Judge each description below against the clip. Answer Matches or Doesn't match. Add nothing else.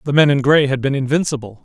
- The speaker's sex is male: Matches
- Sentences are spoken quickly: Matches